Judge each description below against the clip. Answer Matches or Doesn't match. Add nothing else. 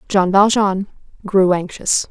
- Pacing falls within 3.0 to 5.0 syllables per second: Matches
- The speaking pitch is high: Matches